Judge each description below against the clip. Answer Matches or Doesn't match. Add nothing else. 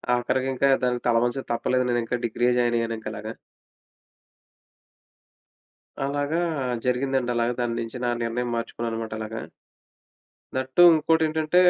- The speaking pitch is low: Matches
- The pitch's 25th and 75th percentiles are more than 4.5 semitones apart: Doesn't match